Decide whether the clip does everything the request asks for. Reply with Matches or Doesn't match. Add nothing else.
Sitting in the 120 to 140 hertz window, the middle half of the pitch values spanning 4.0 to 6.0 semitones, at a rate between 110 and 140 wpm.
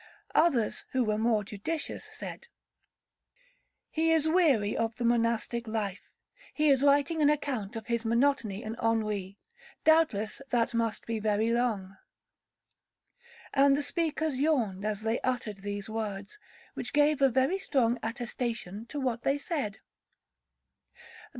Doesn't match